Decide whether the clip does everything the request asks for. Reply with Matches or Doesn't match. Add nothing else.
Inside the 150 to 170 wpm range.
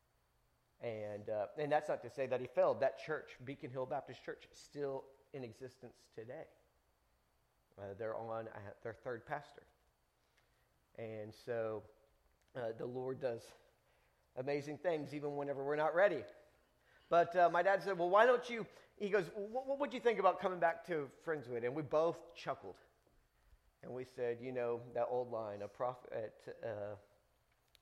Matches